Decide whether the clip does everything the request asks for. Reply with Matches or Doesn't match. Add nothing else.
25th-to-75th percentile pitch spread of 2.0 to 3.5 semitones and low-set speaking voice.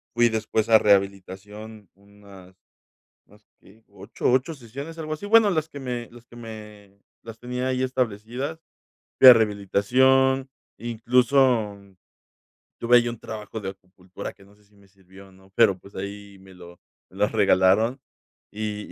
Doesn't match